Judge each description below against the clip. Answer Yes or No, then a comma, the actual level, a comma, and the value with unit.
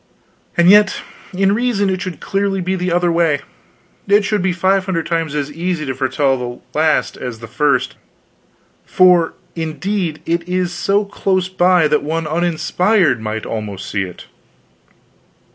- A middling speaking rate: Yes, average, 155 wpm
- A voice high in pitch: No, medium, 170 Hz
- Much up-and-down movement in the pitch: No, average, 4.2 semitones